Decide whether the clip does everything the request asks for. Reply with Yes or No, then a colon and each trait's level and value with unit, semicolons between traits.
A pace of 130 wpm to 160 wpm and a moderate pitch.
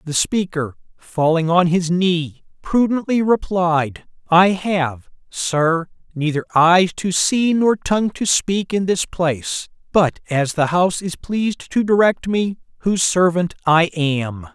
Yes: average, 145 wpm; medium, 180 Hz